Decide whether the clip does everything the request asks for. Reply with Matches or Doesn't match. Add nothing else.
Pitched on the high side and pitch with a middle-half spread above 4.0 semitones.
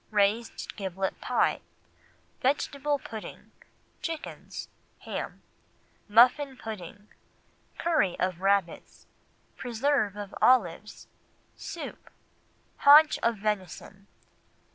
Matches